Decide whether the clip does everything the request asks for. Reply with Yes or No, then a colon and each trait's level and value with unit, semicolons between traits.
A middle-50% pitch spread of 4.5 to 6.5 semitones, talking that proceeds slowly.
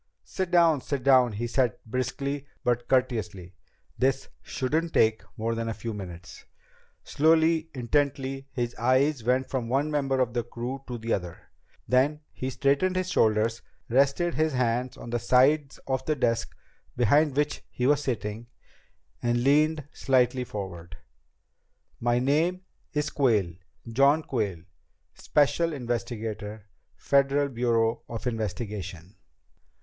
No: average, 3.7 semitones; slow, 130 wpm